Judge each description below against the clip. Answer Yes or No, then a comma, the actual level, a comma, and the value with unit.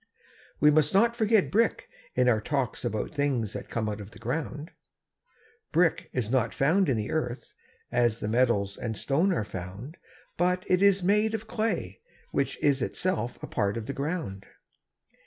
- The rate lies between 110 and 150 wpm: No, average, 175 wpm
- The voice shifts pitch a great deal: Yes, wide, 8.4 semitones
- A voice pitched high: No, medium, 140 Hz